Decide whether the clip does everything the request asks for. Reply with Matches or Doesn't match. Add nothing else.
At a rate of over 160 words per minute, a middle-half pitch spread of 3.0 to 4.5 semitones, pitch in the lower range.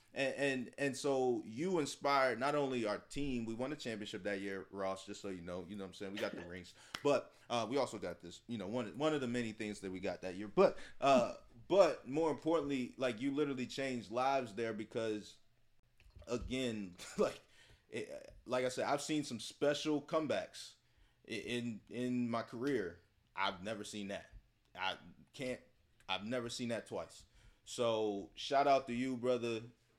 Matches